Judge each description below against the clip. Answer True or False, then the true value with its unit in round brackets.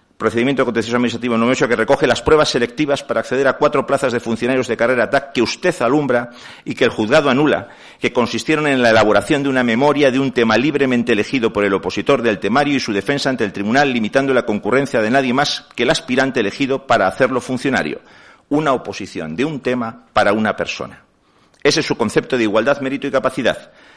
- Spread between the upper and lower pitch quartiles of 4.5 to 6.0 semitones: False (3.2 semitones)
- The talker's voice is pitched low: True (130 Hz)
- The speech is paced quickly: True (205 wpm)